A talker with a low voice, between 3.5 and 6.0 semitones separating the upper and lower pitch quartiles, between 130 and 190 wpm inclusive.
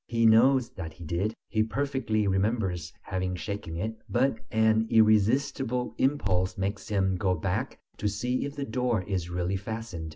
Yes: low, 110 Hz; average, 3.9 semitones; average, 160 wpm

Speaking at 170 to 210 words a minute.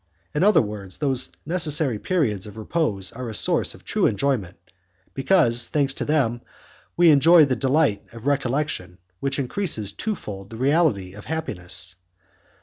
No: average, 145 wpm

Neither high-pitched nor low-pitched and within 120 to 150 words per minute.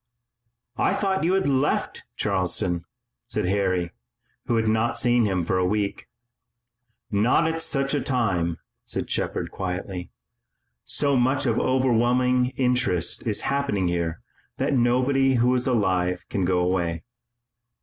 No: low, 115 Hz; slow, 135 wpm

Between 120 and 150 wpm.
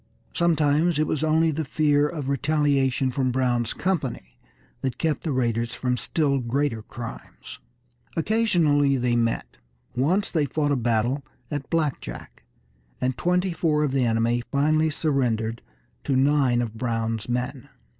Yes: average, 145 wpm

